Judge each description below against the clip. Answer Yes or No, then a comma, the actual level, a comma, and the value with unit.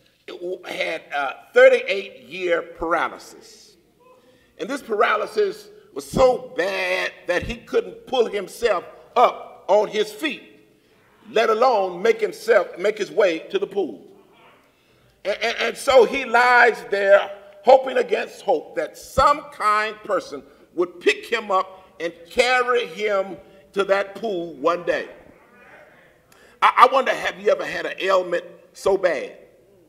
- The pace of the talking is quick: No, slow, 135 wpm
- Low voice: No, very high, 250 Hz